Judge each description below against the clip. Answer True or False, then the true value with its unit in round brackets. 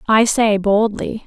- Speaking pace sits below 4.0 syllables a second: True (3.6 syllables/s)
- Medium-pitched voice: False (215 Hz)